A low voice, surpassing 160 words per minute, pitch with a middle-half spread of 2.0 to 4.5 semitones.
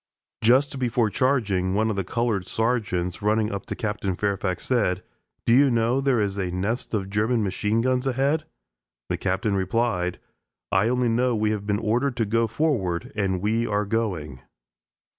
Yes: low, 110 Hz; average, 170 wpm; average, 3.7 semitones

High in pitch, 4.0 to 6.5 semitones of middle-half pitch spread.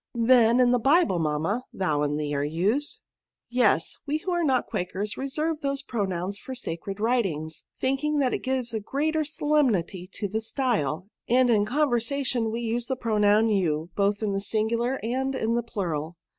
Yes: high, 230 Hz; average, 5.3 semitones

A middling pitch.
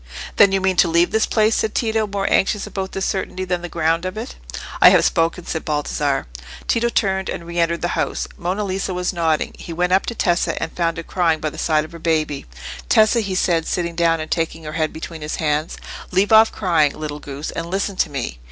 Yes: medium, 170 Hz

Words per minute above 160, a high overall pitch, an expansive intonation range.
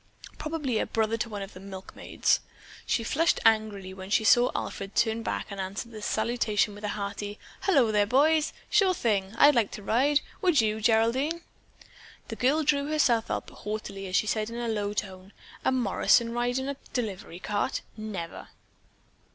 No: average, 175 wpm; high, 220 Hz; average, 3.8 semitones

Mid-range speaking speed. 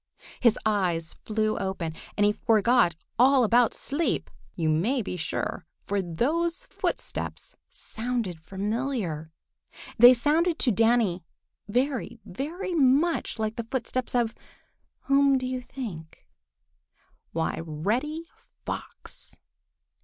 No: slow, 110 wpm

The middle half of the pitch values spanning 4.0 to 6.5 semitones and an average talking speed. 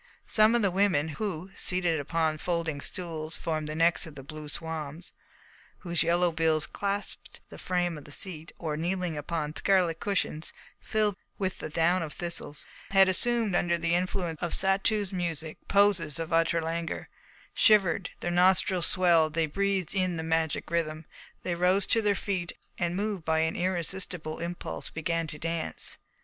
No: average, 2.7 semitones; average, 165 wpm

